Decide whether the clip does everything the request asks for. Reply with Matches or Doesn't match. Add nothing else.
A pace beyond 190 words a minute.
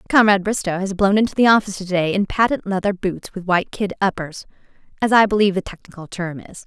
Matches